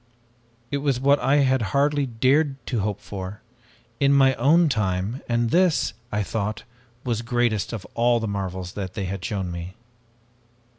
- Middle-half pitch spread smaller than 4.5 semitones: No, wide, 5.4 semitones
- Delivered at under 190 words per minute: Yes, average, 155 wpm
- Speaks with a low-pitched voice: Yes, low, 115 Hz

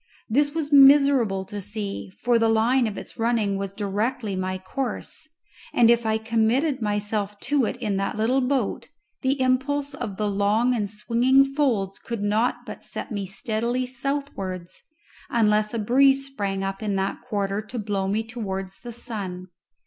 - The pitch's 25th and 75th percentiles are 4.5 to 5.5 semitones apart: No, average, 4.1 semitones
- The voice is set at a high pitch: Yes, high, 220 Hz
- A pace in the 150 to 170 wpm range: Yes, average, 165 wpm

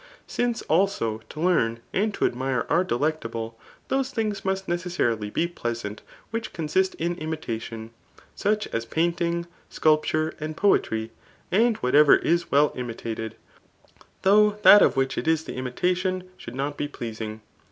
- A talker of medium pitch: Yes, medium, 155 Hz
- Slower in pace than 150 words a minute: Yes, average, 140 wpm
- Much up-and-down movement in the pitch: Yes, wide, 7.8 semitones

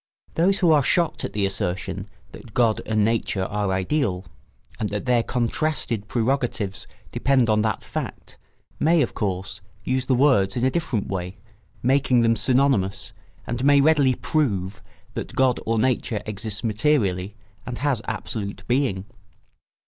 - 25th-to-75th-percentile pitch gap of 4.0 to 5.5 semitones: Yes, average, 5.1 semitones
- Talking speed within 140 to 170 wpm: Yes, average, 150 wpm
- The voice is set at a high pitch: No, low, 115 Hz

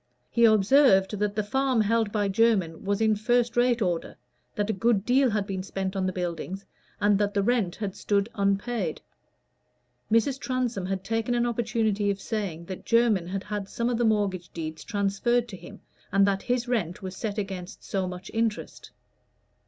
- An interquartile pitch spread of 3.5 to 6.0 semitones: No, average, 3.1 semitones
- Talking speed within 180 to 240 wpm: Yes, average, 185 wpm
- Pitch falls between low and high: No, high, 205 Hz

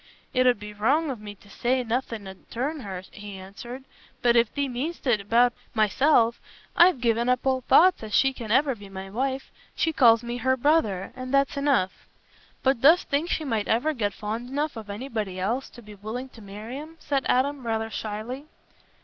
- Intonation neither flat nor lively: Yes, average, 4.1 semitones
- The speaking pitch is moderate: No, high, 240 Hz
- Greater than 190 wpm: Yes, average, 200 wpm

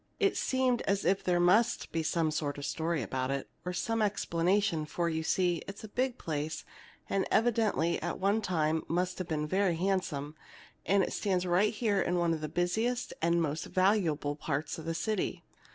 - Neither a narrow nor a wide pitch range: Yes, average, 3.9 semitones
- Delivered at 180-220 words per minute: Yes, average, 185 wpm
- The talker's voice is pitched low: No, medium, 175 Hz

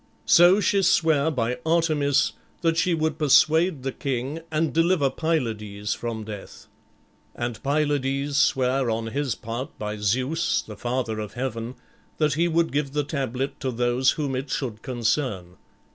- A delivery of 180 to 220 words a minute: No, average, 150 wpm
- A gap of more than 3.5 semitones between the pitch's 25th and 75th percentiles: Yes, average, 4.6 semitones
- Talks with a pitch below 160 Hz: Yes, low, 135 Hz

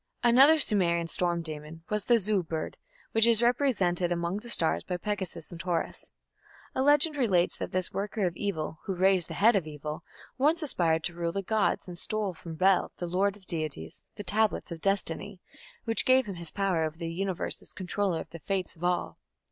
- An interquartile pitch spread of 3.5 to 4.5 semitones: Yes, average, 3.8 semitones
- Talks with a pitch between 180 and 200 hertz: Yes, medium, 185 Hz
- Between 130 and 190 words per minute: No, average, 200 wpm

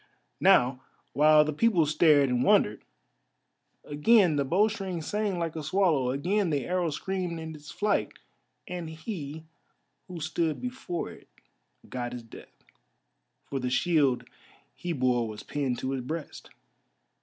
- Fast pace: No, average, 140 wpm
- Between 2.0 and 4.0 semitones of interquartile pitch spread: No, average, 4.7 semitones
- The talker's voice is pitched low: No, medium, 155 Hz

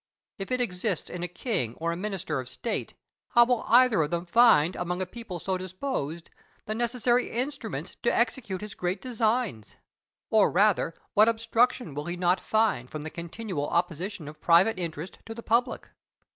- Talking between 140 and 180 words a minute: Yes, average, 170 wpm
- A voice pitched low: No, high, 190 Hz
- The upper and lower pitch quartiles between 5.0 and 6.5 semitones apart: Yes, average, 5.3 semitones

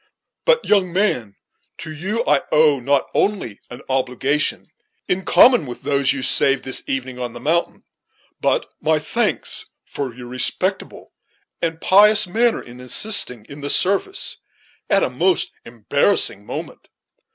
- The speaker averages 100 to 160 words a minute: Yes, average, 140 wpm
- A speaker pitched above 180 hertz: No, medium, 145 Hz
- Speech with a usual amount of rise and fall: No, wide, 7.4 semitones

